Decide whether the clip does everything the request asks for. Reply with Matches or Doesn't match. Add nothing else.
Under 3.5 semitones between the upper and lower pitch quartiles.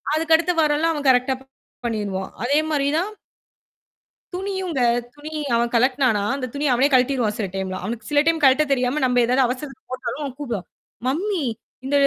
Doesn't match